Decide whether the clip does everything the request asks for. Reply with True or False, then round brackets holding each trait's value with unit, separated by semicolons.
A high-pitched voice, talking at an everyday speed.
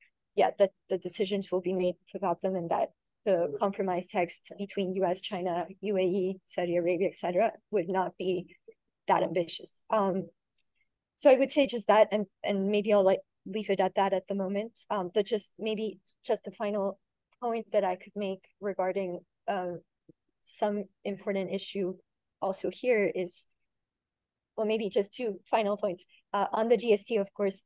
True (195 Hz; 170 wpm)